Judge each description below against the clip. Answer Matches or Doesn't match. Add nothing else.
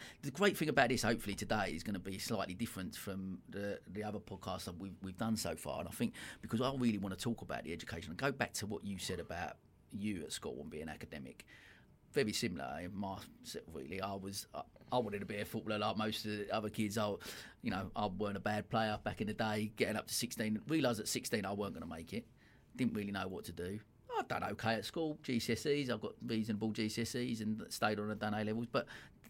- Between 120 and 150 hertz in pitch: Doesn't match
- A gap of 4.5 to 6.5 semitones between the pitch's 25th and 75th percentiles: Doesn't match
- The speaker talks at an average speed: Doesn't match